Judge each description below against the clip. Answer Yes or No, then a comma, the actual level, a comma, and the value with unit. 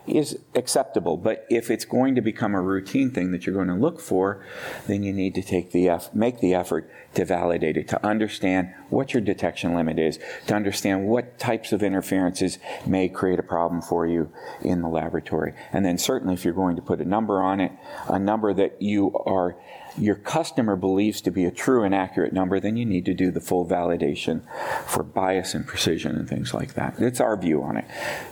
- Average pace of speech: No, fast, 210 wpm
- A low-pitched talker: Yes, very low, 95 Hz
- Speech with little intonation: Yes, narrow, 2.3 semitones